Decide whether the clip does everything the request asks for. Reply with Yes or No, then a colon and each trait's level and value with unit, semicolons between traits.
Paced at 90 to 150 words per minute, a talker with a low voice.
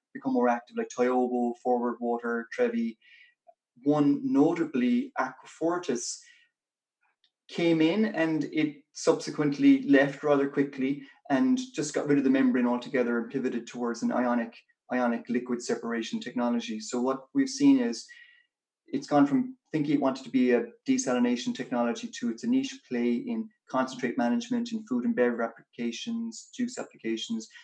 No: average, 145 wpm; medium, 145 Hz